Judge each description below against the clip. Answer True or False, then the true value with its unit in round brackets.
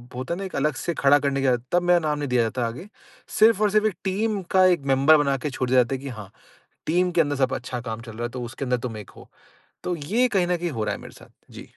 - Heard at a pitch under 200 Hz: True (140 Hz)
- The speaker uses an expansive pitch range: True (5.8 semitones)